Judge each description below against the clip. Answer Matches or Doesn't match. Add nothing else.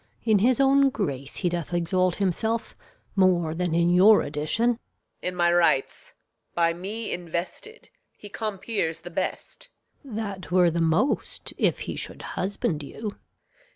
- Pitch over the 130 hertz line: Matches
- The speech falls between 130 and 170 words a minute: Matches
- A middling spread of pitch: Matches